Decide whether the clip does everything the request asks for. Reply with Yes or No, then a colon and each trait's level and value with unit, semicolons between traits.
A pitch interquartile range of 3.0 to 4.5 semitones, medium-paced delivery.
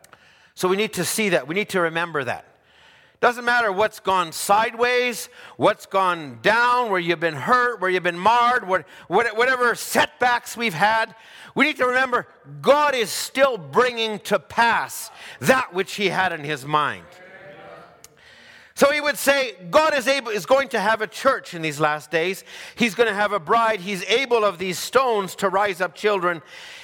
No: average, 5.0 semitones; average, 180 wpm